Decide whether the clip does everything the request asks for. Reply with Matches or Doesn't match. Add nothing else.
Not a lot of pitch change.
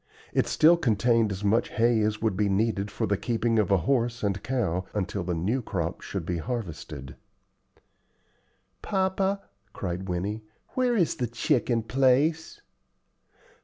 Doesn't match